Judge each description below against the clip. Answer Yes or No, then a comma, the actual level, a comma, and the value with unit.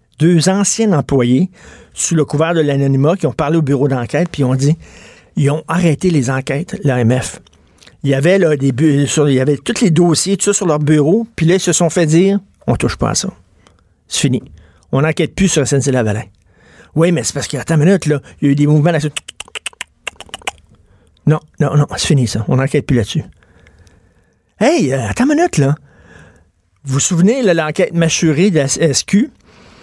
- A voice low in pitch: No, medium, 150 Hz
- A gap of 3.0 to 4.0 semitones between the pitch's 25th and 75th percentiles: No, average, 4.4 semitones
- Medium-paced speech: Yes, average, 205 wpm